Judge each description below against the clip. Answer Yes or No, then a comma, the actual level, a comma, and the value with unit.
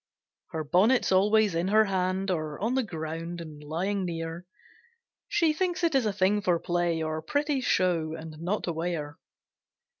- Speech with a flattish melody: No, average, 4.3 semitones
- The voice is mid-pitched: Yes, medium, 180 Hz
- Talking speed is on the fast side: No, average, 170 wpm